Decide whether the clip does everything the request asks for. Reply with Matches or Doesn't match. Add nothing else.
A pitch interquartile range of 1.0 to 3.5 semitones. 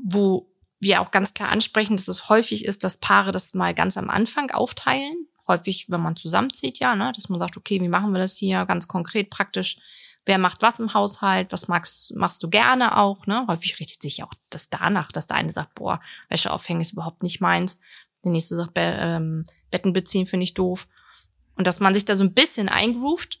Matches